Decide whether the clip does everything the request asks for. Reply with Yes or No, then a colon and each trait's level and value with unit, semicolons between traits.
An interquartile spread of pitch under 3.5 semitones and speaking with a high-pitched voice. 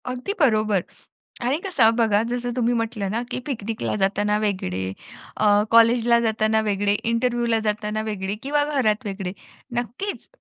Yes: narrow, 2.6 semitones; high, 225 Hz